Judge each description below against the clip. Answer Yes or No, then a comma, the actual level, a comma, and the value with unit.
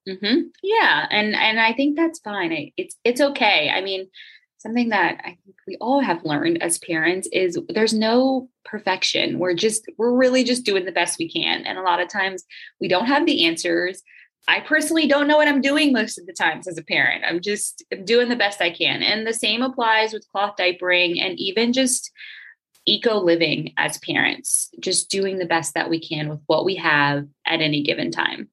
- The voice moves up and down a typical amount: No, wide, 7.5 semitones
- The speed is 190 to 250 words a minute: Yes, fast, 205 wpm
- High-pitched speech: Yes, high, 215 Hz